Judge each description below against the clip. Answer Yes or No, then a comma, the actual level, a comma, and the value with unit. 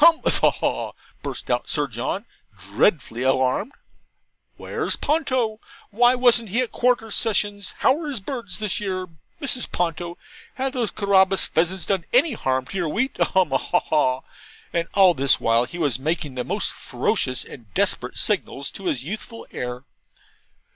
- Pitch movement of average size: No, wide, 8.5 semitones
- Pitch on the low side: No, high, 190 Hz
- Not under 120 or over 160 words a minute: No, average, 175 wpm